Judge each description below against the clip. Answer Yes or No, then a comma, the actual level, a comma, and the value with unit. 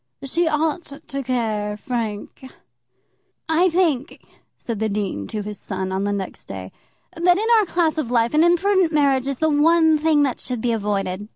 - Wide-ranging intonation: Yes, wide, 7.3 semitones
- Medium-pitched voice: No, very high, 265 Hz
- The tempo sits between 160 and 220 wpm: Yes, average, 180 wpm